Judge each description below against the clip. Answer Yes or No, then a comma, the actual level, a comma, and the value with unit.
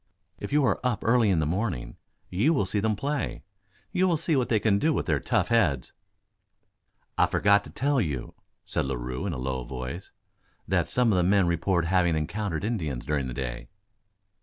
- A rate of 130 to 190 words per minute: No, average, 200 wpm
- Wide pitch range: Yes, wide, 7.8 semitones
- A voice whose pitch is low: Yes, very low, 95 Hz